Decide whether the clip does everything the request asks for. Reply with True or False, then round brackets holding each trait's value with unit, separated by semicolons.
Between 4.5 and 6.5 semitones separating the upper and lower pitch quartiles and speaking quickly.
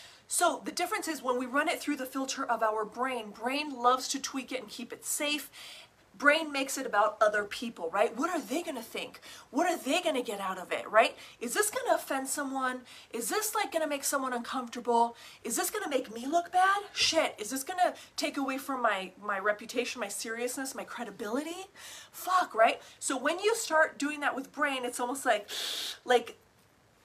True (5.2 semitones; 215 wpm)